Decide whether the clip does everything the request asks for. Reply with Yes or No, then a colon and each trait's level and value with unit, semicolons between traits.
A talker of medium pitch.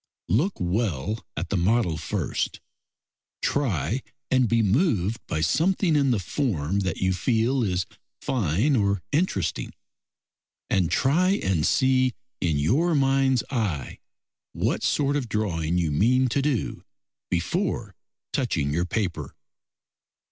No: low, 110 Hz